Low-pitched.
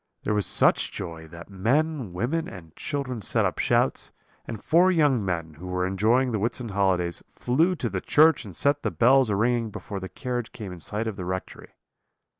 Yes: low, 110 Hz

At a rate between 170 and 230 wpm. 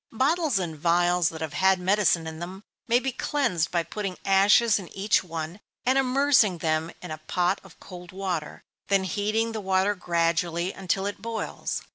Yes: average, 180 wpm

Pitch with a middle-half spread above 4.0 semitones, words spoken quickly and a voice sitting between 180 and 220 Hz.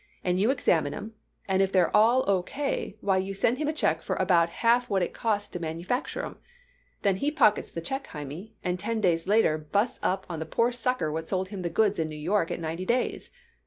Yes: average, 5.1 semitones; fast, 230 wpm; high, 190 Hz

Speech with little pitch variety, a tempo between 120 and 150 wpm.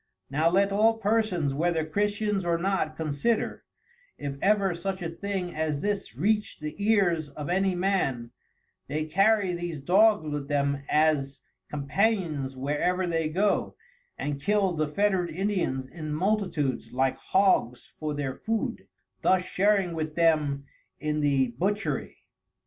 No: average, 5.1 semitones; average, 140 wpm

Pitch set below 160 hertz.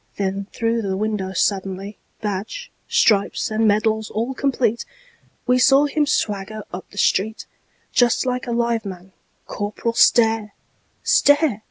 No: high, 220 Hz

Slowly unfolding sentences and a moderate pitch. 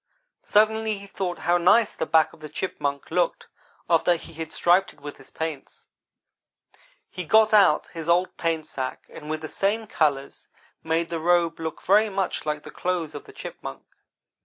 No: average, 180 wpm; medium, 170 Hz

